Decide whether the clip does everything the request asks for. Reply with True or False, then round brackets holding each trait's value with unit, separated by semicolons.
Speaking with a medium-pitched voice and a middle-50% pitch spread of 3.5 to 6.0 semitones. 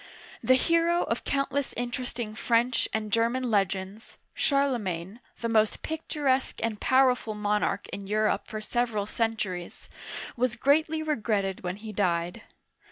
False (230 Hz; 3.9 semitones)